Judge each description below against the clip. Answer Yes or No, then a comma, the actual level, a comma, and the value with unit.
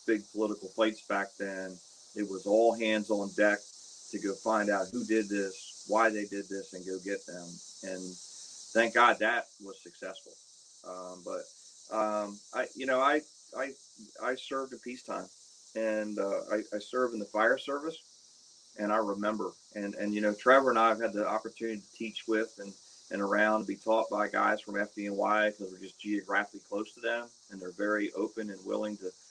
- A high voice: No, low, 105 Hz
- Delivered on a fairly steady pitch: Yes, narrow, 1.9 semitones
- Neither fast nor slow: Yes, average, 190 wpm